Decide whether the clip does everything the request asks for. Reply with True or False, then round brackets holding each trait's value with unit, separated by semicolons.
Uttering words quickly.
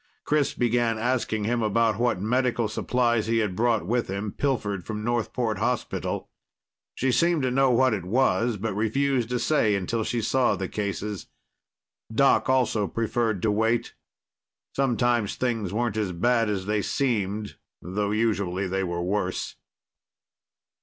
False (145 wpm)